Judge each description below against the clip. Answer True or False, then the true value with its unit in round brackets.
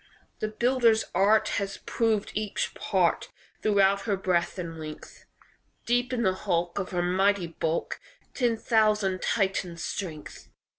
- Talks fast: False (135 wpm)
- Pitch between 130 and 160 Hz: False (195 Hz)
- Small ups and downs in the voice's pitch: False (3.6 semitones)